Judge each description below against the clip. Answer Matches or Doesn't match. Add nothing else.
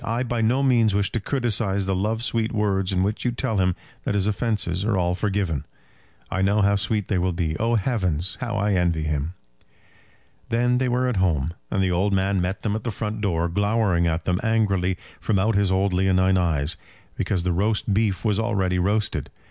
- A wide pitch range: Doesn't match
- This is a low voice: Matches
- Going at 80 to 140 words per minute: Doesn't match